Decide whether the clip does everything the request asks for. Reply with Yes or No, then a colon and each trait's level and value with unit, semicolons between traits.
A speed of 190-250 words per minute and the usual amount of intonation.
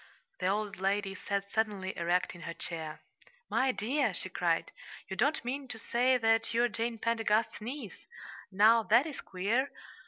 No: average, 160 wpm; average, 3.6 semitones